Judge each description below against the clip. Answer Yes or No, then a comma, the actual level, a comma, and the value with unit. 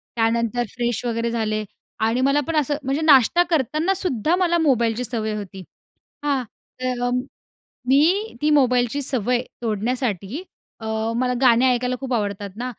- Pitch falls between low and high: No, very high, 250 Hz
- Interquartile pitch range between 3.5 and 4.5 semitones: Yes, average, 3.9 semitones